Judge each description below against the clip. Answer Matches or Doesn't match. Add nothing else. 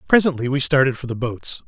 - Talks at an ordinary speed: Doesn't match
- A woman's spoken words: Doesn't match